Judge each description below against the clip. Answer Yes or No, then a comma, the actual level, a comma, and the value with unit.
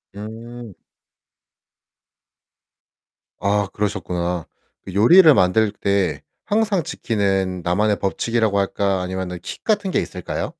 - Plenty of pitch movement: No, average, 3.5 semitones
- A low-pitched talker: Yes, low, 100 Hz